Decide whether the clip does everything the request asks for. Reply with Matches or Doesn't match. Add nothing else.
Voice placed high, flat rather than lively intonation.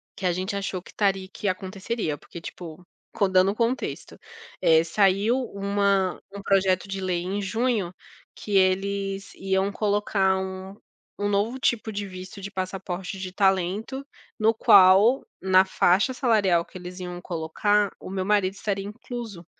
Matches